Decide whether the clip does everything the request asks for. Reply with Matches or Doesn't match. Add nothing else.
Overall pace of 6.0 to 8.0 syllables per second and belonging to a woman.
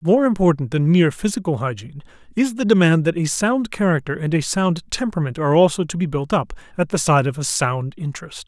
Doesn't match